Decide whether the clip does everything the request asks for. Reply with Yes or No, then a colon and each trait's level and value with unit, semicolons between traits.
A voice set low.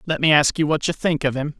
No: medium, 150 Hz